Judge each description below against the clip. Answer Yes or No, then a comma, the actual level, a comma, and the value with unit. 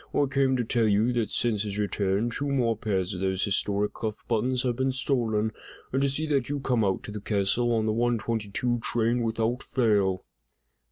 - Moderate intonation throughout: Yes, average, 3.2 semitones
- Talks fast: Yes, fast, 210 wpm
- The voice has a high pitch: No, low, 115 Hz